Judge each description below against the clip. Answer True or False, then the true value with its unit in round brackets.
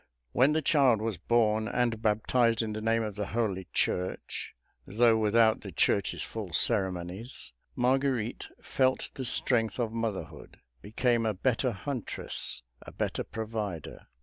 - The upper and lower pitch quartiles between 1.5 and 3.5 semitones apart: True (2.7 semitones)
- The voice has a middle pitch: False (110 Hz)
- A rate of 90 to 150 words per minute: True (140 wpm)